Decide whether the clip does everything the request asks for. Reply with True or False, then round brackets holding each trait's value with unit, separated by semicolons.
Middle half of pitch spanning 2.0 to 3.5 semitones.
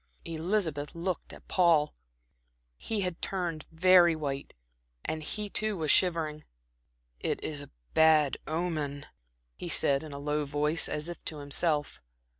True (2.8 semitones)